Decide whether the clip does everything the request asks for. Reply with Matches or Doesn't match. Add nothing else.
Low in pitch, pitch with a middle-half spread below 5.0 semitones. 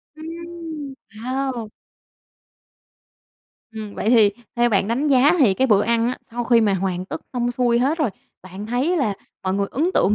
Doesn't match